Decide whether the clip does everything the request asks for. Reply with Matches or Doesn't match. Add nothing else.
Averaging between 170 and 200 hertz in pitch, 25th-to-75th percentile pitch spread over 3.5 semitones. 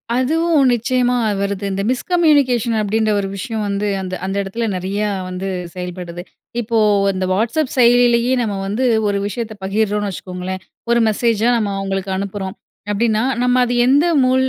Doesn't match